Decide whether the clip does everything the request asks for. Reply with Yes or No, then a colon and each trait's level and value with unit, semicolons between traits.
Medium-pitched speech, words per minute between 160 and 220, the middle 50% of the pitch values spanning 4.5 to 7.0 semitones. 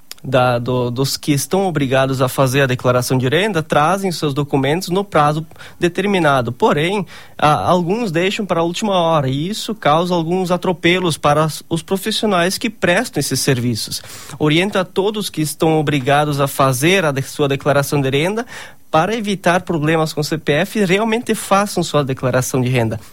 Yes: medium, 155 Hz; average, 165 wpm; average, 5.1 semitones